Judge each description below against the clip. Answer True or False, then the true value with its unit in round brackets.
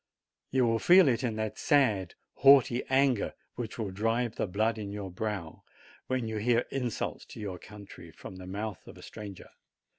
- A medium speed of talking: True (180 wpm)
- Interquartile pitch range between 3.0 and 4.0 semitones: True (3.4 semitones)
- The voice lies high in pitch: False (110 Hz)